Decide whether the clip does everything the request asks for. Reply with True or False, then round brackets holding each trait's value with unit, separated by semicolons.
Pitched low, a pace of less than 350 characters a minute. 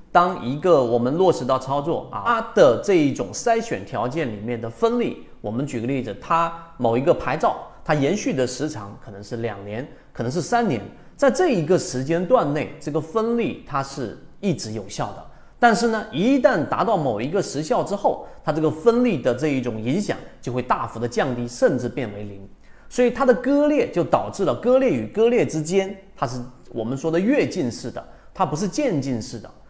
False (150 Hz; 290 characters per minute)